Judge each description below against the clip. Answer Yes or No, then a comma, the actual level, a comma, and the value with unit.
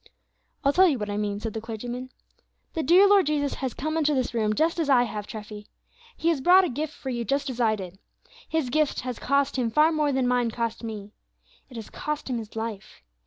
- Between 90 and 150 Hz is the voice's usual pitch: No, very high, 250 Hz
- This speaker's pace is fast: Yes, fast, 235 wpm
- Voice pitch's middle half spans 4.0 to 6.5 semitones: Yes, average, 5.3 semitones